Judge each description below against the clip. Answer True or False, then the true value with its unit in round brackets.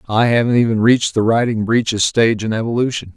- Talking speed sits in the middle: True (190 wpm)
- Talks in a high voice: False (115 Hz)